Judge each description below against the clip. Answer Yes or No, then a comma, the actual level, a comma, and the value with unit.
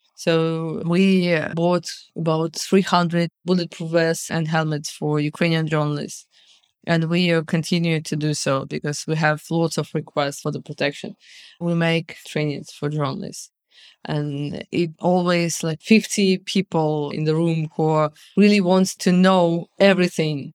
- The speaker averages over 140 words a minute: No, slow, 135 wpm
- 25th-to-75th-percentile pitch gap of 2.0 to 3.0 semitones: Yes, narrow, 2.5 semitones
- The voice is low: No, medium, 165 Hz